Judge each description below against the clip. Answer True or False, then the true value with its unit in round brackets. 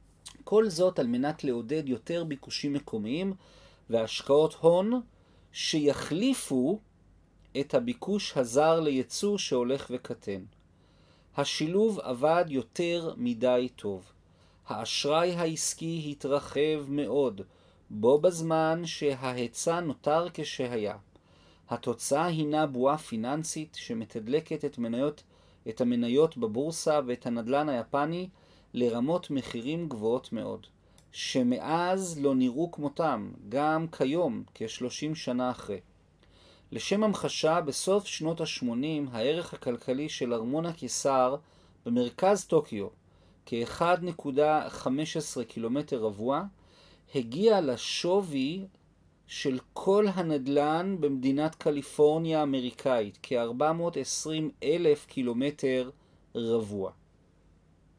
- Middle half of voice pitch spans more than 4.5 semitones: True (5.3 semitones)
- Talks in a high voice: False (145 Hz)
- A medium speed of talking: False (85 wpm)